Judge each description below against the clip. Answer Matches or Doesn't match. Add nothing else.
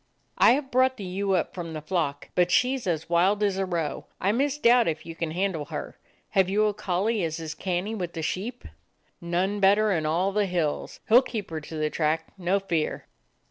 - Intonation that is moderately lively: Matches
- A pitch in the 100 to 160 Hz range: Doesn't match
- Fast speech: Matches